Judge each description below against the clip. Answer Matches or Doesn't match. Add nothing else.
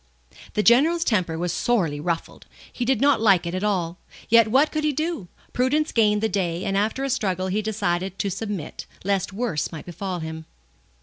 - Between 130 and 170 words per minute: Doesn't match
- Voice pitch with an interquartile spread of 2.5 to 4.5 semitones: Doesn't match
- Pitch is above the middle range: Matches